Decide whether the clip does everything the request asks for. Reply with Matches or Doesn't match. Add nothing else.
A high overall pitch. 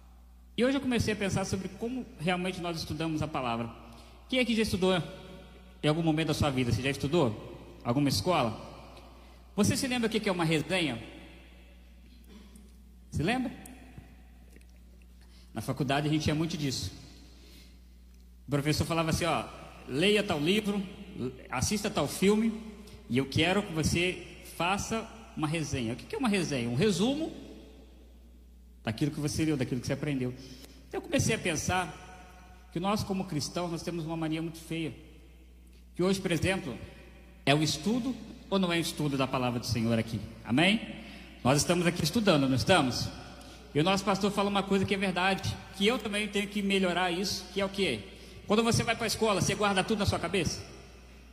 Doesn't match